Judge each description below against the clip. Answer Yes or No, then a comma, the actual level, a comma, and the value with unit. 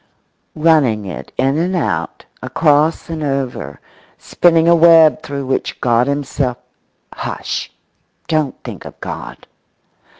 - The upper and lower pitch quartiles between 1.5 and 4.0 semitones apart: Yes, average, 3.7 semitones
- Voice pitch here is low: No, medium, 145 Hz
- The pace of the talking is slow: Yes, slow, 110 wpm